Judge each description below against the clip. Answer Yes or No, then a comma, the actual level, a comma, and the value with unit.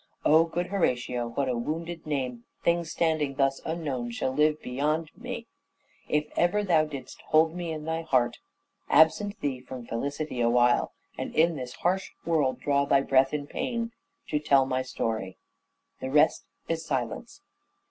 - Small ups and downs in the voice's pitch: No, average, 3.9 semitones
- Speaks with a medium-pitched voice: Yes, medium, 150 Hz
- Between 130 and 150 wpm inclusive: No, average, 160 wpm